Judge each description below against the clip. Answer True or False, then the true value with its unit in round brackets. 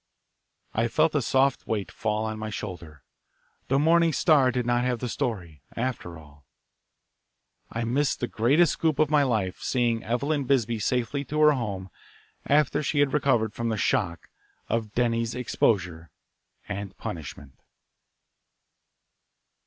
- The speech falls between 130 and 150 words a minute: True (140 wpm)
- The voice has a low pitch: True (120 Hz)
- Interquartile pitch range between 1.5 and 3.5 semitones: False (4.8 semitones)